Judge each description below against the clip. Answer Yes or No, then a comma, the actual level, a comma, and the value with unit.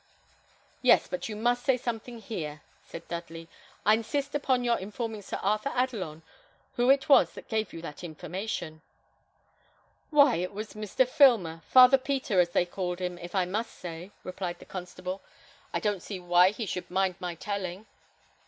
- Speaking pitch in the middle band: No, high, 200 Hz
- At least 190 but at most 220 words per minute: No, average, 170 wpm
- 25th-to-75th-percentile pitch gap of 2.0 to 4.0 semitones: No, average, 5.2 semitones